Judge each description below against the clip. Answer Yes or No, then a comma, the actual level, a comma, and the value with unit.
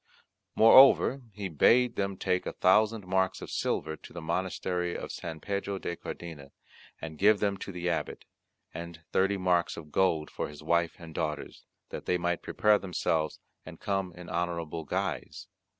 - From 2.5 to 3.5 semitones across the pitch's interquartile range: Yes, average, 2.9 semitones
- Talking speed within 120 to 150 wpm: No, average, 165 wpm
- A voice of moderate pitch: No, very low, 90 Hz